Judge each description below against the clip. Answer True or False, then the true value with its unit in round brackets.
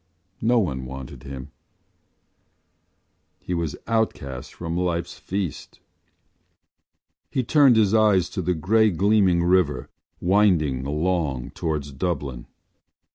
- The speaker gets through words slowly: True (105 wpm)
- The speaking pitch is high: False (85 Hz)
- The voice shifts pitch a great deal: True (6.2 semitones)